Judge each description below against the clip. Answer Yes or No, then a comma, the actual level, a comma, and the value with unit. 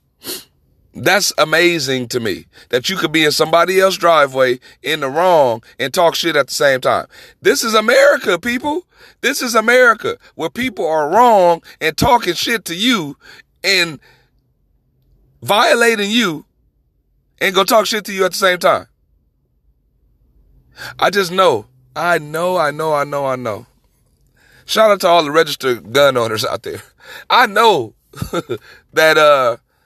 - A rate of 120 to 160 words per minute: Yes, average, 155 wpm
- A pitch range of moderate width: No, wide, 7.1 semitones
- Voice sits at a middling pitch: Yes, medium, 170 Hz